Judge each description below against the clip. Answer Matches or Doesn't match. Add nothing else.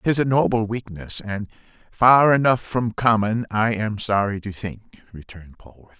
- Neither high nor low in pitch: Doesn't match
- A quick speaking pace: Doesn't match